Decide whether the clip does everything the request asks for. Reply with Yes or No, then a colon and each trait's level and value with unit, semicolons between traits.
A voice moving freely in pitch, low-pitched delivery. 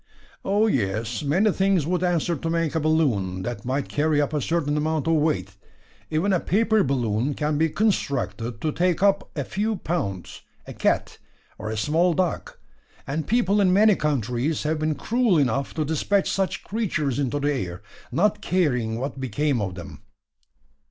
No: wide, 5.8 semitones; medium, 155 Hz